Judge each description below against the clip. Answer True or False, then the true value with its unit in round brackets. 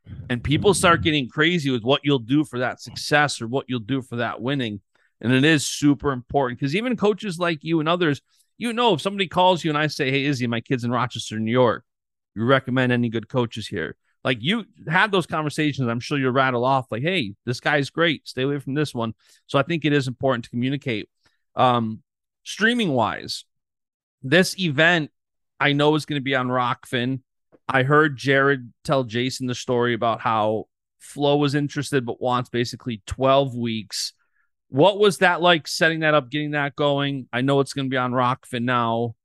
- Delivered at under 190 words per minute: False (200 wpm)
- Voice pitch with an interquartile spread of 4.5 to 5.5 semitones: False (3.6 semitones)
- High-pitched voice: False (135 Hz)